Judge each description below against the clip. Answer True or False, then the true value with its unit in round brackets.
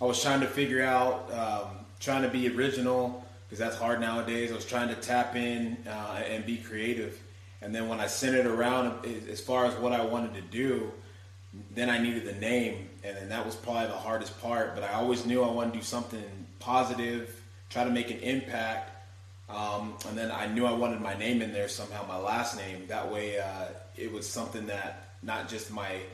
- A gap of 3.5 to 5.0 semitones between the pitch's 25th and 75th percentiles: False (2.8 semitones)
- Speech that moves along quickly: True (215 wpm)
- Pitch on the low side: True (115 Hz)